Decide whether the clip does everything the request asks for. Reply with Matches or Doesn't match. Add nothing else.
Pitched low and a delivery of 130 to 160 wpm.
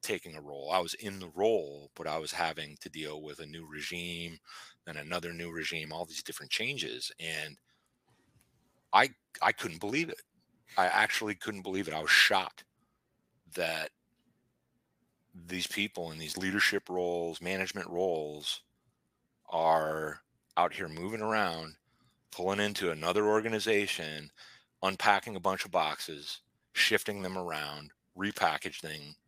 Matches